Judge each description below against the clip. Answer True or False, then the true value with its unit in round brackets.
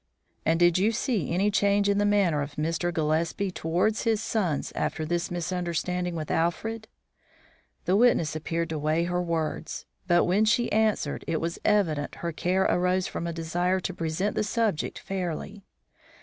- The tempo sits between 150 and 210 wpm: True (165 wpm)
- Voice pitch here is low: False (175 Hz)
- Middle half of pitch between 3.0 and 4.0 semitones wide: True (3.5 semitones)